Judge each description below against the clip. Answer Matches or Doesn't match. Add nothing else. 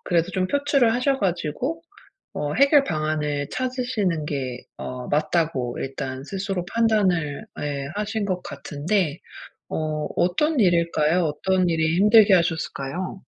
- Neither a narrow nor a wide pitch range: Doesn't match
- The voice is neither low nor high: Matches